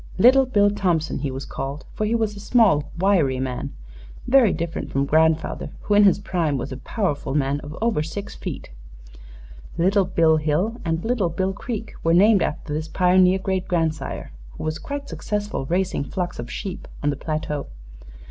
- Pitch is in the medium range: Yes, medium, 175 Hz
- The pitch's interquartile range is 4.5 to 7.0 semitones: Yes, average, 5.2 semitones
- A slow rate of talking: No, average, 175 wpm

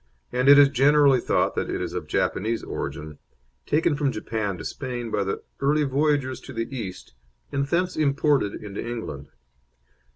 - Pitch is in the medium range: No, low, 130 Hz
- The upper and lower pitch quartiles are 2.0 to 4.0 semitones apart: No, average, 4.6 semitones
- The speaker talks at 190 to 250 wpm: No, average, 165 wpm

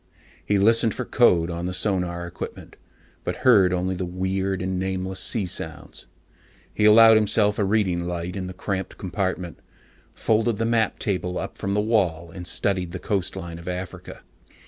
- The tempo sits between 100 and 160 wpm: No, average, 170 wpm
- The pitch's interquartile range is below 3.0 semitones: Yes, narrow, 2.6 semitones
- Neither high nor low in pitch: No, very low, 95 Hz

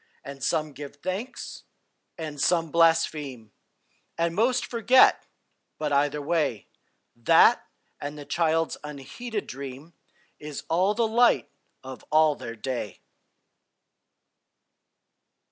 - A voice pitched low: No, medium, 155 Hz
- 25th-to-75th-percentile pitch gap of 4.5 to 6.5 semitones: No, average, 3.7 semitones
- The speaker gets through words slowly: Yes, slow, 105 wpm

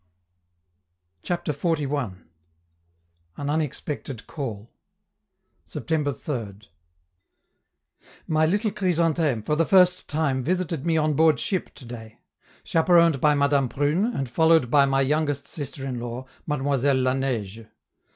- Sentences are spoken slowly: Yes, slow, 120 wpm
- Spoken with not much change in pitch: No, average, 3.6 semitones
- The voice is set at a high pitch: No, medium, 145 Hz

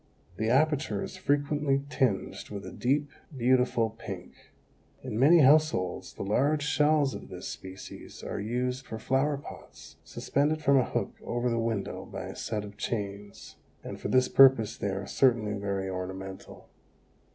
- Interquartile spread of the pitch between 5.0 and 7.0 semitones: Yes, wide, 5.4 semitones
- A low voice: Yes, low, 125 Hz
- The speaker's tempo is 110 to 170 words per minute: Yes, average, 155 wpm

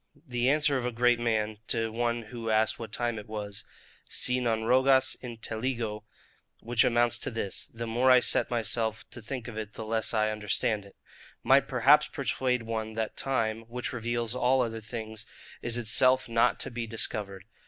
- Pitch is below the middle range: Yes, low, 115 Hz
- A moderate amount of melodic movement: No, narrow, 1.8 semitones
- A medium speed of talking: Yes, average, 175 wpm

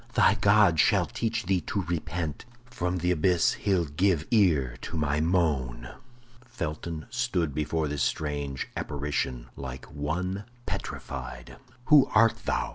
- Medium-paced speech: No, slow, 130 wpm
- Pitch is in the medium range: No, very low, 80 Hz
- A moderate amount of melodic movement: Yes, average, 4.6 semitones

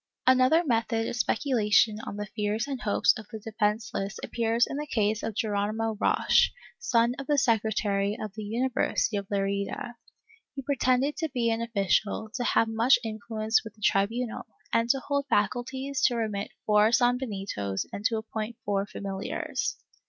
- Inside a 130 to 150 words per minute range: No, average, 165 wpm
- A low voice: No, high, 225 Hz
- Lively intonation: No, average, 2.9 semitones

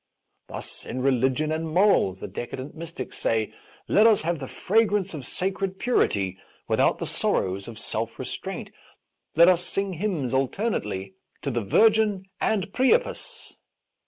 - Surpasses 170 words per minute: No, average, 145 wpm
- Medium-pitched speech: Yes, medium, 165 Hz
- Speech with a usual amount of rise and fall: No, wide, 7.9 semitones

